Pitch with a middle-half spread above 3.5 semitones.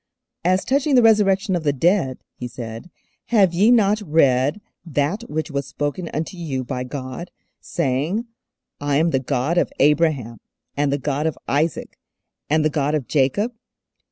Yes: average, 5.1 semitones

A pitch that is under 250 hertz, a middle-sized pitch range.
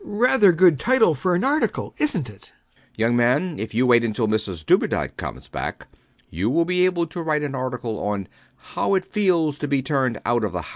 No: medium, 140 Hz; wide, 7.6 semitones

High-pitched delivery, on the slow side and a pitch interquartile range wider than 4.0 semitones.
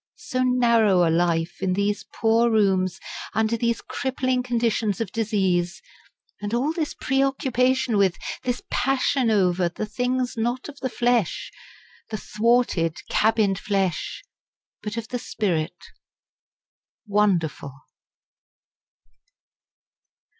Yes: high, 220 Hz; slow, 110 wpm; average, 4.6 semitones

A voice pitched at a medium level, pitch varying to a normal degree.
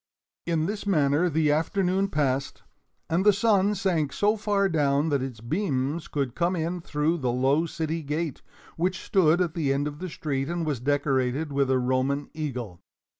Yes: medium, 155 Hz; average, 4.1 semitones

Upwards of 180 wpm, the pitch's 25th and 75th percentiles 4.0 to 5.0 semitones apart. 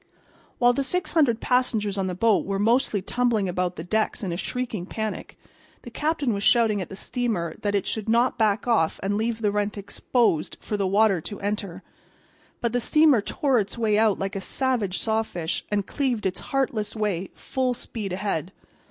No: average, 190 wpm; average, 3.6 semitones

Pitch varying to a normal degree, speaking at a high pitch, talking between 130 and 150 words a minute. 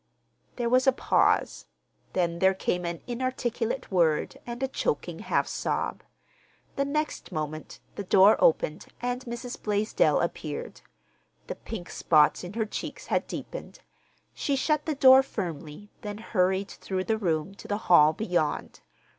No: wide, 6.0 semitones; high, 210 Hz; average, 145 wpm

